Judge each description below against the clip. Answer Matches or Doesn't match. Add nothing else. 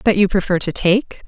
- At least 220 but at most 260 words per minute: Matches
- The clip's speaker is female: Matches